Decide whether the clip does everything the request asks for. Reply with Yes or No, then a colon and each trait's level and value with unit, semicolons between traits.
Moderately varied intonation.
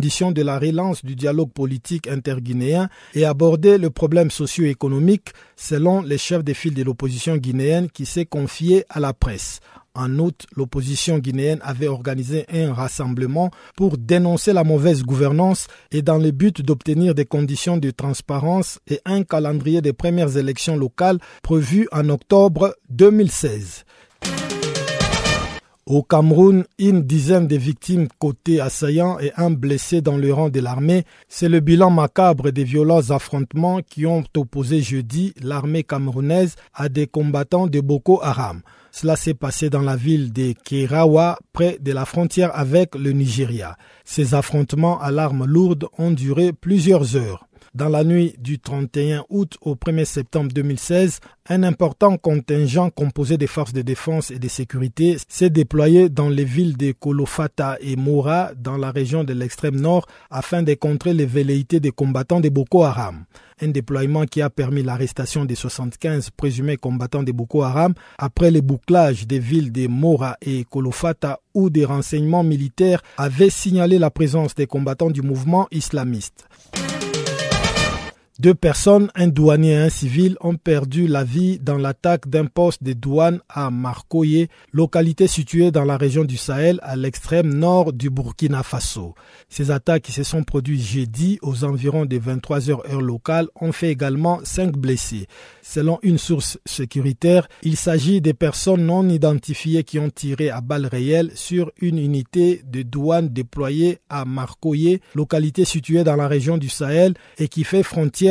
Yes: average, 3.6 semitones